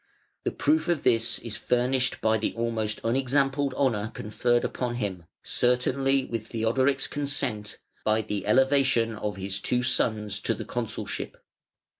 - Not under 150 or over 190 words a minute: No, average, 140 wpm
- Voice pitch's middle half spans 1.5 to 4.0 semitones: Yes, average, 3.6 semitones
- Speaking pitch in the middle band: No, low, 120 Hz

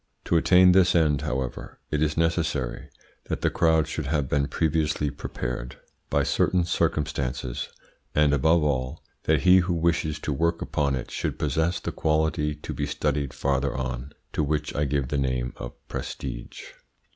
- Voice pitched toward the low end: Yes, very low, 75 Hz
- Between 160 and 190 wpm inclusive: Yes, average, 165 wpm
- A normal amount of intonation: Yes, average, 3.1 semitones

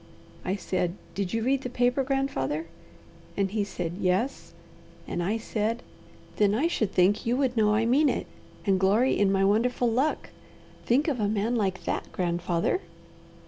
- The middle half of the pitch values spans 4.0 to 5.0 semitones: Yes, average, 4.4 semitones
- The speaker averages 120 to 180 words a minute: Yes, average, 170 wpm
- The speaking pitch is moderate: No, high, 215 Hz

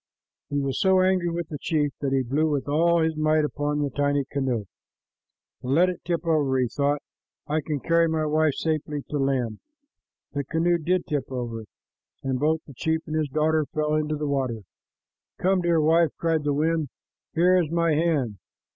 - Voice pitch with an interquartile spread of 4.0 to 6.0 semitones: No, narrow, 2.6 semitones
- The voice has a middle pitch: Yes, medium, 155 Hz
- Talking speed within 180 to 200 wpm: Yes, average, 185 wpm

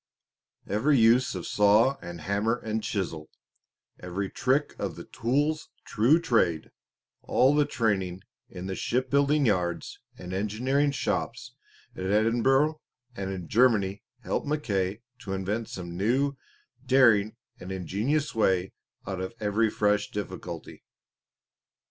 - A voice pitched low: Yes, low, 105 Hz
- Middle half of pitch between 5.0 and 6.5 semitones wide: Yes, average, 5.3 semitones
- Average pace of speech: No, slow, 125 wpm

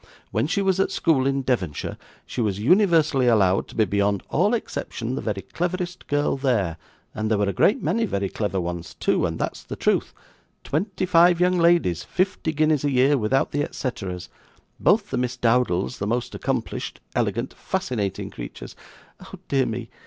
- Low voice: Yes, low, 130 Hz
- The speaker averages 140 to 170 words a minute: No, average, 180 wpm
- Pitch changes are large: Yes, wide, 8.6 semitones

